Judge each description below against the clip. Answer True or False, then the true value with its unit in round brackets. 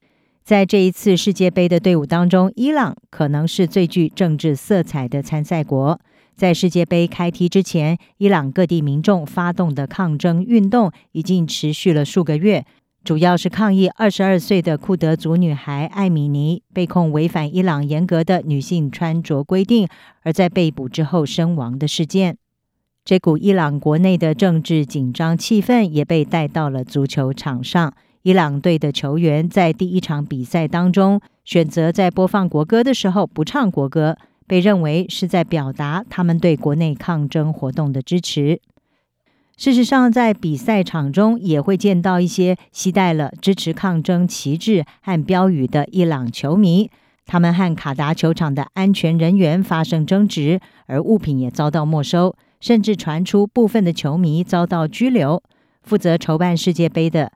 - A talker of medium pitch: True (170 Hz)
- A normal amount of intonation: True (3.4 semitones)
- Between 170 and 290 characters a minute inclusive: True (255 characters per minute)